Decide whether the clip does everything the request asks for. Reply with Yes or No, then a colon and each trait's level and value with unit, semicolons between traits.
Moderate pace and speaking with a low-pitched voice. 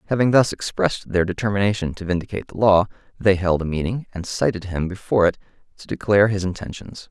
Yes: average, 185 wpm; very low, 95 Hz